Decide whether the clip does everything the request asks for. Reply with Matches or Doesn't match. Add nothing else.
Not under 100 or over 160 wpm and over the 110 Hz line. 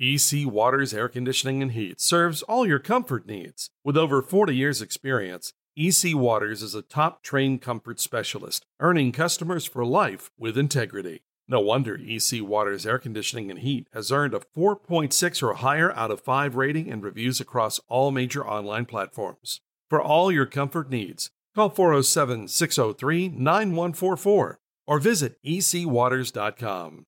Matches